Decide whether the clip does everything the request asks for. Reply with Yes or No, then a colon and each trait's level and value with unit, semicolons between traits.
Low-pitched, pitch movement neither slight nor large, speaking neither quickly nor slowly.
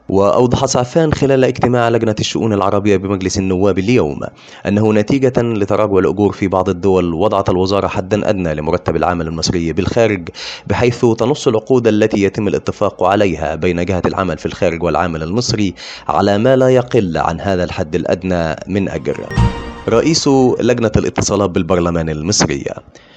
No: low, 100 Hz; average, 4.2 semitones; fast, 140 wpm